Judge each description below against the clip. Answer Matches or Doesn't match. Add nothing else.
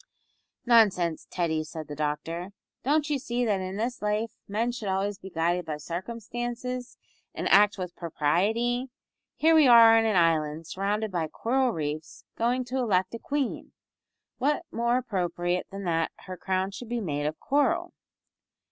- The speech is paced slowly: Doesn't match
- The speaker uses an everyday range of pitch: Doesn't match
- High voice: Matches